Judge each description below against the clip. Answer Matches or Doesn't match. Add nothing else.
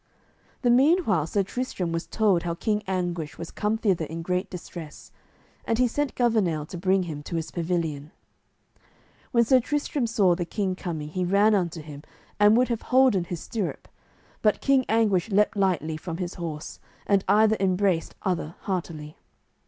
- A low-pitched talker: Doesn't match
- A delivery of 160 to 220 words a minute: Matches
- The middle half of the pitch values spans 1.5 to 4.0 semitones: Doesn't match